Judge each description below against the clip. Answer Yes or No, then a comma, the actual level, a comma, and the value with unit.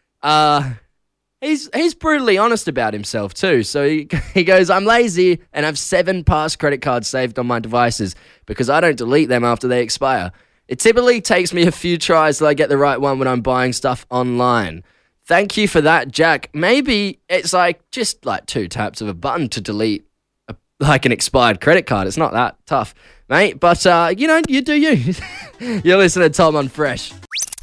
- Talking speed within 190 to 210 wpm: Yes, average, 200 wpm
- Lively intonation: Yes, wide, 6.9 semitones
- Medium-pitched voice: Yes, medium, 155 Hz